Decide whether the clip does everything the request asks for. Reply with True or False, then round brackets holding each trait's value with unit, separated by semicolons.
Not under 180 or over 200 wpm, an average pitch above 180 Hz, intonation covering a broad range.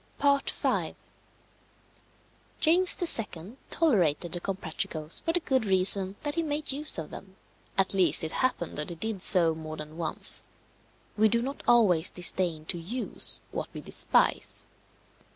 False (145 wpm; 190 Hz; 7.9 semitones)